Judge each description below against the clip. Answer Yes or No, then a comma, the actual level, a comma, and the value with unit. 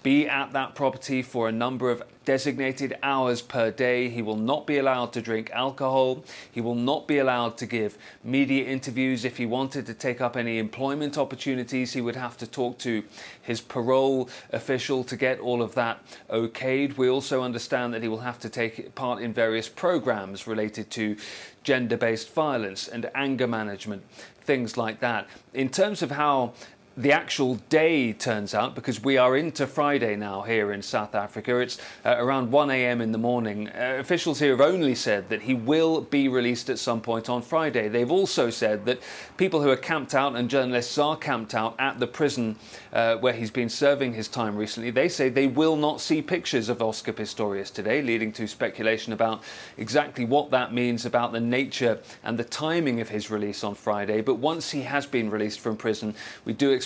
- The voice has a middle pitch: No, low, 125 Hz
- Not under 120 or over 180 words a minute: No, average, 195 wpm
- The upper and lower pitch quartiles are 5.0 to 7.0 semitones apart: No, average, 3.0 semitones